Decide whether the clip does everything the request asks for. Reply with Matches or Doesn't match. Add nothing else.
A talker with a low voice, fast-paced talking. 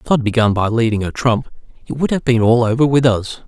Matches